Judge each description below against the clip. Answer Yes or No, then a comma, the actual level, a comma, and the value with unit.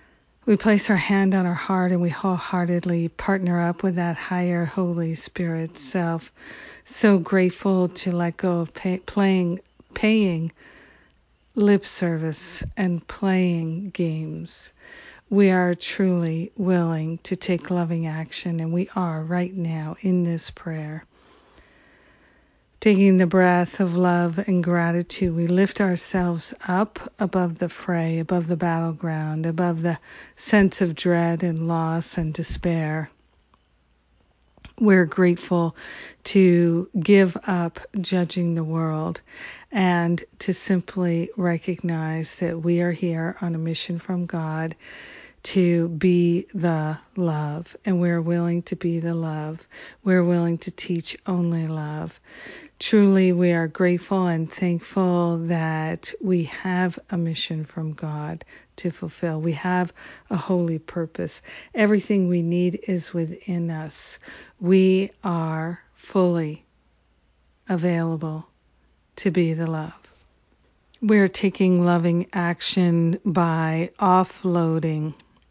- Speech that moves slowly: Yes, slow, 120 wpm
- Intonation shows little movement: Yes, narrow, 2.0 semitones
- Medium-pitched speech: Yes, medium, 175 Hz